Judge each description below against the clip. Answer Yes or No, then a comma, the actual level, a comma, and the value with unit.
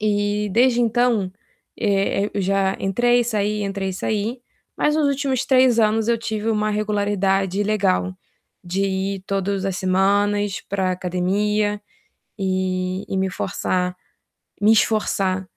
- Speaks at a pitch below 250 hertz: Yes, high, 205 Hz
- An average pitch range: No, narrow, 2.1 semitones